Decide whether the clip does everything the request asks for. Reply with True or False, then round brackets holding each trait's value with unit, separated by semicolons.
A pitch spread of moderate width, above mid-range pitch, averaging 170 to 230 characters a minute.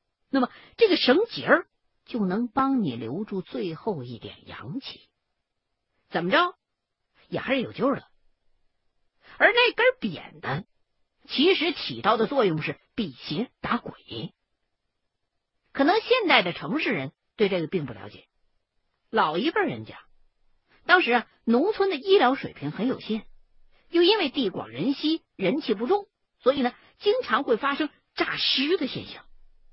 False (8.9 semitones; 275 Hz; 205 characters per minute)